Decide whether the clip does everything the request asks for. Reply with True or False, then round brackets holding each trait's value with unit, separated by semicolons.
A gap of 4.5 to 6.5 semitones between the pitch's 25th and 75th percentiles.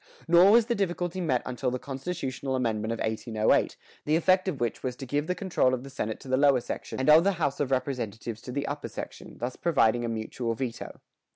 True (5.4 semitones)